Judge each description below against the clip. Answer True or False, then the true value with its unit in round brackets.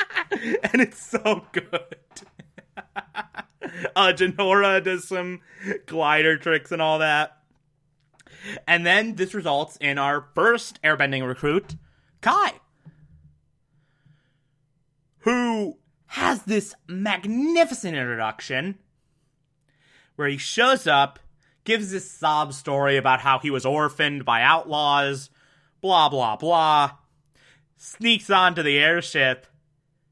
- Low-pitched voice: False (155 Hz)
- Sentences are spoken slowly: True (100 wpm)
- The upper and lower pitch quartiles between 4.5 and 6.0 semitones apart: True (4.9 semitones)